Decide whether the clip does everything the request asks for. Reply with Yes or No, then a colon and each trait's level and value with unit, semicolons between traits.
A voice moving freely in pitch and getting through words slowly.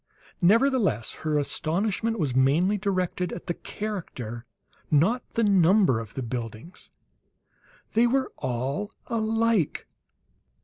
Yes: wide, 8.5 semitones; slow, 105 wpm